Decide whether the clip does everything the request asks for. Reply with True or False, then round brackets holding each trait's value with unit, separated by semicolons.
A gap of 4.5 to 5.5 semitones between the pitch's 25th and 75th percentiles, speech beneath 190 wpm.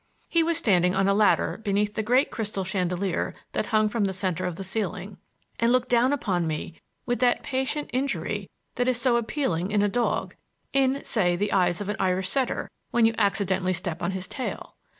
False (4.8 semitones; 195 wpm)